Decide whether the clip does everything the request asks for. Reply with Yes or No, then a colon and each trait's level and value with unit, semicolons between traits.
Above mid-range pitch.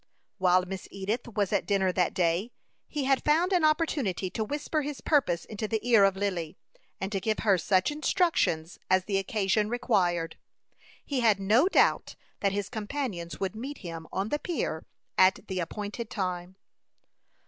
Yes: high, 205 Hz